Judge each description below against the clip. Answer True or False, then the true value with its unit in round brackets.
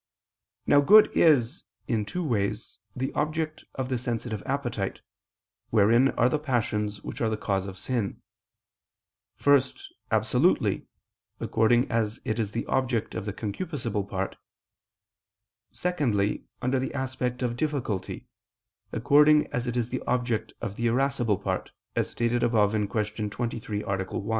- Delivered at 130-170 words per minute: True (140 wpm)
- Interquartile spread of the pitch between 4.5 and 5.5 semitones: False (3.9 semitones)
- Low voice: True (120 Hz)